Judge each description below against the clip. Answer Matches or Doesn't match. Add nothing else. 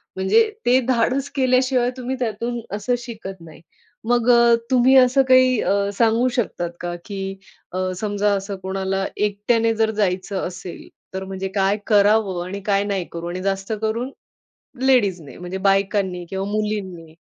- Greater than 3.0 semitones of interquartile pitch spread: Matches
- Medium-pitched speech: Doesn't match